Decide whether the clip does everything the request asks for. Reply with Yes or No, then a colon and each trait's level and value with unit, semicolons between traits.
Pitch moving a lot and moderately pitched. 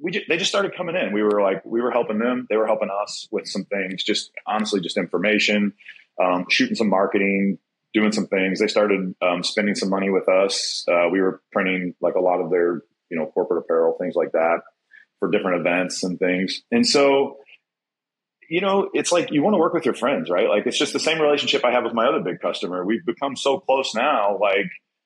No: wide, 7.5 semitones; low, 110 Hz